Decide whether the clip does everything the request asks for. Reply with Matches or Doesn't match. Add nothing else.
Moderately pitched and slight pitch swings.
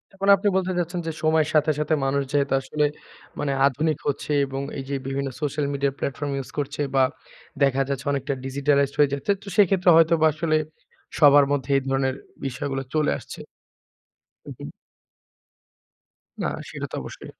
Matches